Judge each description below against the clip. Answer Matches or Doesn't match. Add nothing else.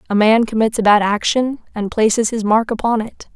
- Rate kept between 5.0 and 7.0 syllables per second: Matches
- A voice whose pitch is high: Matches